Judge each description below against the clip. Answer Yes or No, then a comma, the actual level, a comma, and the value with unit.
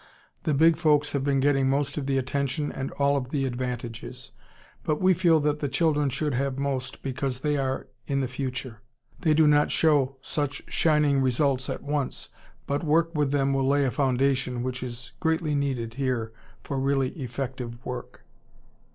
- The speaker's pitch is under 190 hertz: Yes, low, 135 Hz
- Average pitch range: No, narrow, 2.2 semitones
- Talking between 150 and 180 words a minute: Yes, average, 175 wpm